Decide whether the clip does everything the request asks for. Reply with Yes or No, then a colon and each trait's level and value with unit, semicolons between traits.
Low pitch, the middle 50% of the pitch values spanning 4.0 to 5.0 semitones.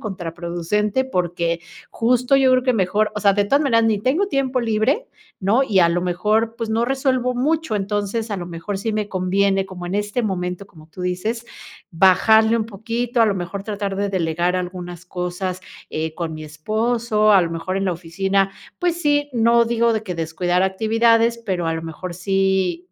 No: high, 200 Hz; average, 4.3 semitones